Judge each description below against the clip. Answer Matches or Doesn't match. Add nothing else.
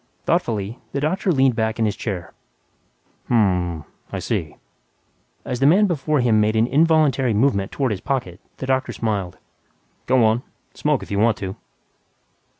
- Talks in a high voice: Doesn't match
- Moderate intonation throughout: Matches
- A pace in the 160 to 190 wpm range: Matches